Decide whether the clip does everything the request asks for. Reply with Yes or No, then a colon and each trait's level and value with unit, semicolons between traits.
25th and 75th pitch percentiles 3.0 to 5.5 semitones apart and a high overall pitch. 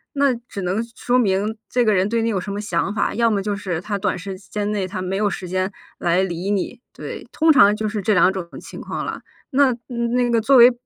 Yes: average, 3.6 semitones; high, 205 Hz